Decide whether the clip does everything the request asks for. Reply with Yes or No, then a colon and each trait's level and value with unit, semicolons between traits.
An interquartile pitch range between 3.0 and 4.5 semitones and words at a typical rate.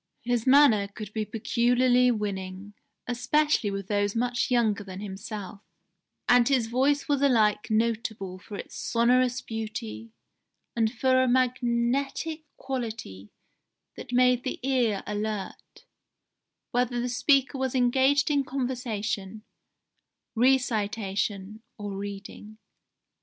No: average, 3.6 semitones; slow, 110 wpm